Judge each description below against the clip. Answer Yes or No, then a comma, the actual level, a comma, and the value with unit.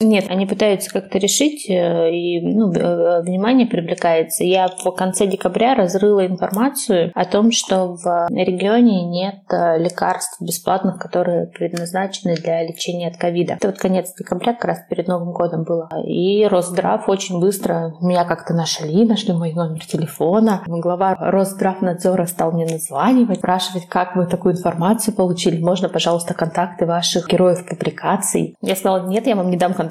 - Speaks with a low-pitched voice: No, medium, 180 Hz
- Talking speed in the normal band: Yes, average, 150 wpm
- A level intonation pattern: Yes, narrow, 2.1 semitones